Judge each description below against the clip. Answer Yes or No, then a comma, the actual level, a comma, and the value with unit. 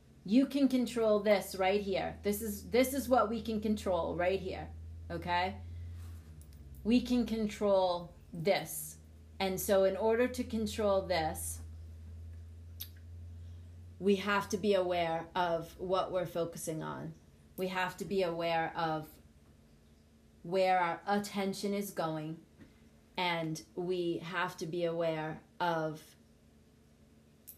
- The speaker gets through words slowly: Yes, slow, 120 wpm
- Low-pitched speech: No, medium, 170 Hz